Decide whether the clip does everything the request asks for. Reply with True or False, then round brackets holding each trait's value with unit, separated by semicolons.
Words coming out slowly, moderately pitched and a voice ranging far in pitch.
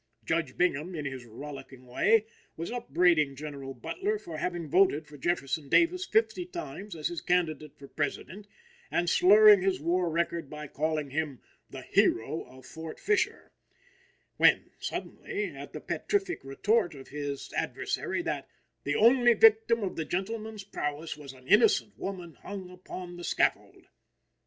False (150 wpm; 170 Hz; 6.1 semitones)